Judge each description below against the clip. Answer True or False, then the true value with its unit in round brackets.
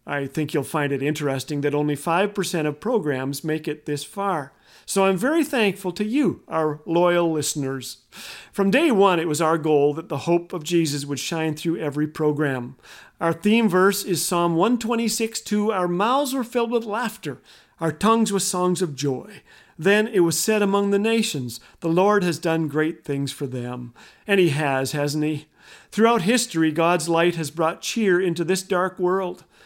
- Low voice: False (170 Hz)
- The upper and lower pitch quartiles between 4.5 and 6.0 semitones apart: True (5.1 semitones)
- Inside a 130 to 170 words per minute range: False (185 wpm)